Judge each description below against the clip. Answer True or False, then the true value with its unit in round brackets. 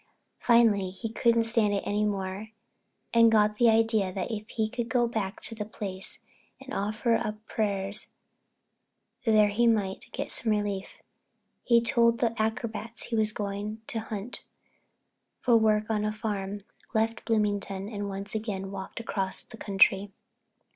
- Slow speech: False (155 wpm)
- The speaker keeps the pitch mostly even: True (2.1 semitones)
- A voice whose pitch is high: True (215 Hz)